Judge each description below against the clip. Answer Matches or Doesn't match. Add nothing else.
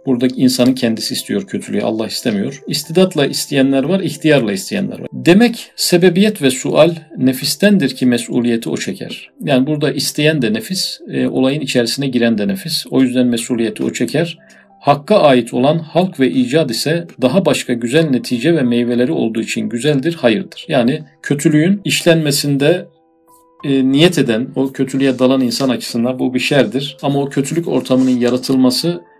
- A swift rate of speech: Matches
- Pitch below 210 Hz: Matches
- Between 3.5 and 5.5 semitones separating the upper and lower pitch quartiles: Matches